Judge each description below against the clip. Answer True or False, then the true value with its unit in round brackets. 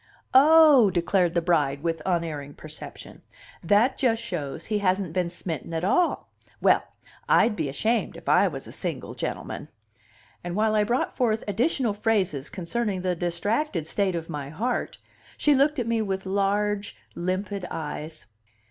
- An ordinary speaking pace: True (155 wpm)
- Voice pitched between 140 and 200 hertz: True (190 Hz)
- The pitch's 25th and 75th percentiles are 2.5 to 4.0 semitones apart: False (4.9 semitones)